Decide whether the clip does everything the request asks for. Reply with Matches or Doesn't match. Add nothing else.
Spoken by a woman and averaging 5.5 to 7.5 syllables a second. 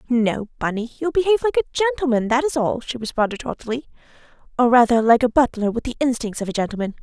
Matches